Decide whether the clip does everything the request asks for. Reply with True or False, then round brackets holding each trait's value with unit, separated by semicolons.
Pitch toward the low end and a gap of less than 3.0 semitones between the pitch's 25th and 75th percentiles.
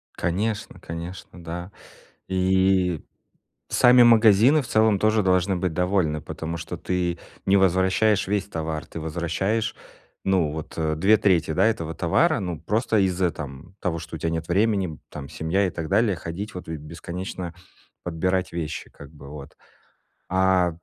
False (90 Hz; 3.3 semitones)